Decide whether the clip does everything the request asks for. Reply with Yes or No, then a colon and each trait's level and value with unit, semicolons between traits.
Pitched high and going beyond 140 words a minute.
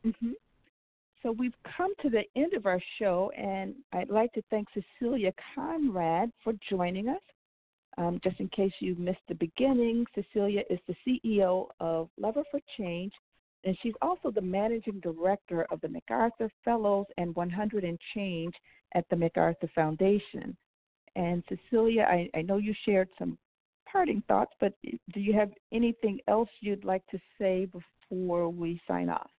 Yes: high, 200 Hz; average, 160 wpm